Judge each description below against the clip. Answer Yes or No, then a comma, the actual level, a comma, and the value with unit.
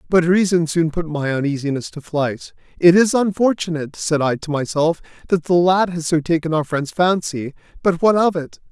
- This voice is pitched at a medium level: Yes, medium, 165 Hz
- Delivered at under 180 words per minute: No, average, 195 wpm